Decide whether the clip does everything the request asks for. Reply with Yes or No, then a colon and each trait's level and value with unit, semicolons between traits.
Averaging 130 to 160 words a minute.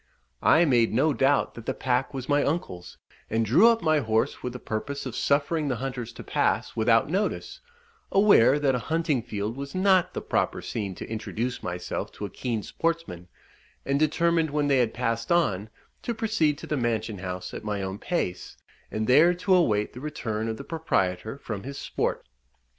No: average, 190 wpm